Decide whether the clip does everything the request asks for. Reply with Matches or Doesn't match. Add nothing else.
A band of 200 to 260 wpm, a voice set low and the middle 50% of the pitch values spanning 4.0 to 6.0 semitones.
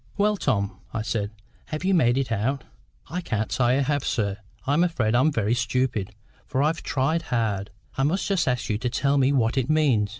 Matches